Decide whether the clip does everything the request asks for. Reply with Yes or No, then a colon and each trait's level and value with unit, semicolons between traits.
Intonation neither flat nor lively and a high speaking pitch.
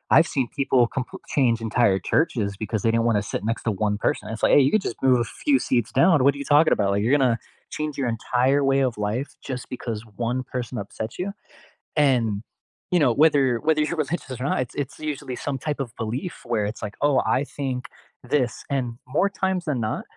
No: average, 3.9 semitones; low, 130 Hz